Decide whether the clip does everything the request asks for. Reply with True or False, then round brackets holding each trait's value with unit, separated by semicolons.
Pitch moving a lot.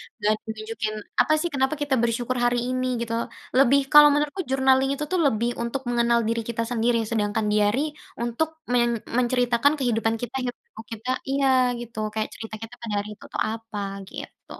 False (2.8 semitones)